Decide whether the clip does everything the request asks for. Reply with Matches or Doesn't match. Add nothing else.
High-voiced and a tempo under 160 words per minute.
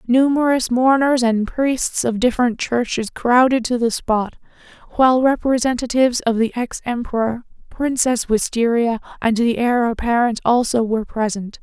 Matches